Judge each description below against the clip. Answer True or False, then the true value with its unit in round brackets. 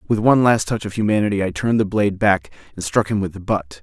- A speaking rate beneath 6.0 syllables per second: False (6.5 syllables/s)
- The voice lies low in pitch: True (100 Hz)